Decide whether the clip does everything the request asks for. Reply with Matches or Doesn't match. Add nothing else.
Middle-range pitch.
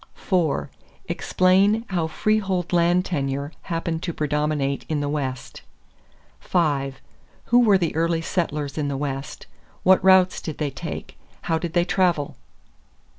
Matches